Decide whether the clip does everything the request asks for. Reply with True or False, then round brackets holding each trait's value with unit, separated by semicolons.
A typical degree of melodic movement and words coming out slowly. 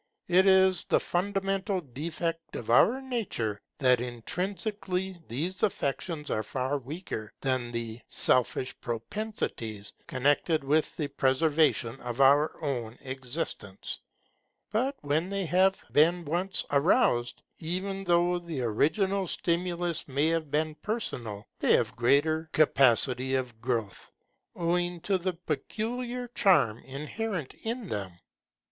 False (6.5 semitones; 120 wpm)